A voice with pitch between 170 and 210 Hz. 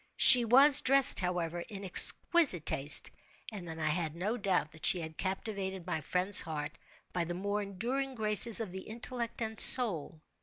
Yes: high, 190 Hz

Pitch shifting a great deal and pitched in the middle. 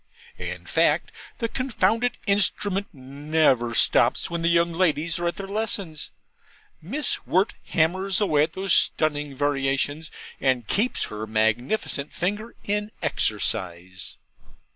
Yes: wide, 6.4 semitones; medium, 165 Hz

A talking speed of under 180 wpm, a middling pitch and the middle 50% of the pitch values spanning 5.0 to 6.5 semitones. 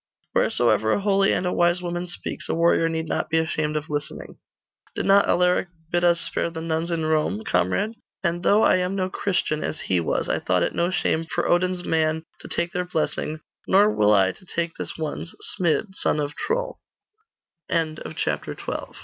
No: average, 160 wpm; medium, 170 Hz; average, 2.7 semitones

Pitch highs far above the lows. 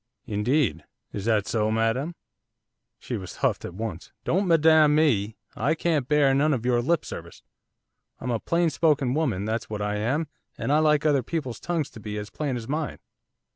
Yes: wide, 5.8 semitones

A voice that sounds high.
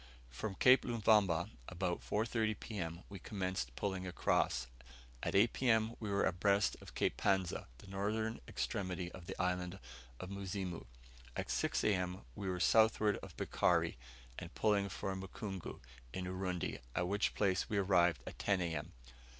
No: very low, 95 Hz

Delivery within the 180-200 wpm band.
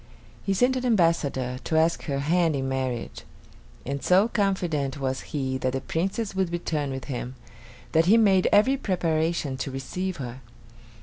No: average, 165 wpm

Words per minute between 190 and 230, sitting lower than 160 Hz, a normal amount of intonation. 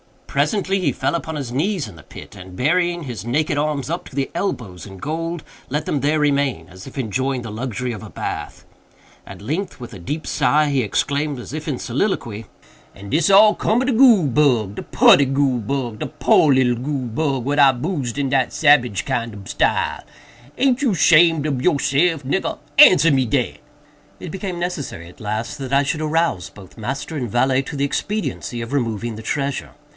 Yes: average, 200 wpm; medium, 140 Hz; average, 4.6 semitones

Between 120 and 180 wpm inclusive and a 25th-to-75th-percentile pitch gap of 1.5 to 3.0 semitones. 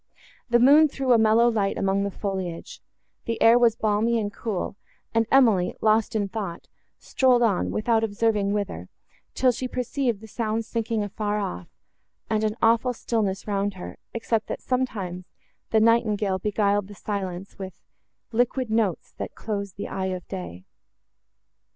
Yes: average, 155 wpm; average, 2.7 semitones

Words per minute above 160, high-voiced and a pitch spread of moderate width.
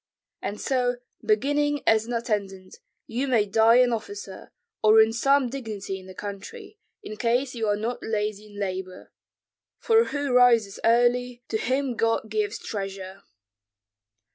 No: average, 145 wpm; high, 225 Hz; average, 3.4 semitones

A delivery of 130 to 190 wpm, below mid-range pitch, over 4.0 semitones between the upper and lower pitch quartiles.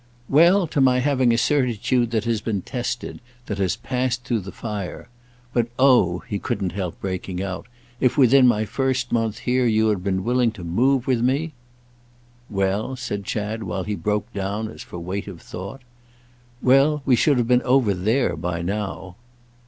Yes: average, 175 wpm; low, 115 Hz; average, 4.4 semitones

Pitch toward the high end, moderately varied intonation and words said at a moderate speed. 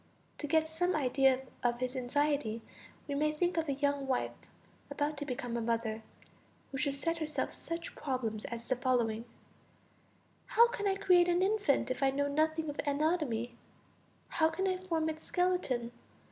Yes: very high, 290 Hz; average, 4.5 semitones; average, 170 wpm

